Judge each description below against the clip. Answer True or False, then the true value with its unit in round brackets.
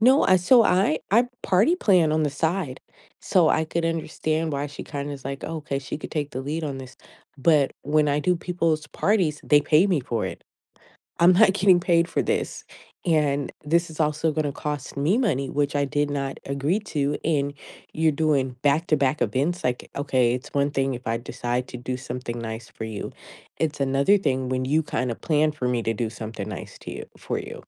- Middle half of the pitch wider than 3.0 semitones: True (3.7 semitones)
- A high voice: False (145 Hz)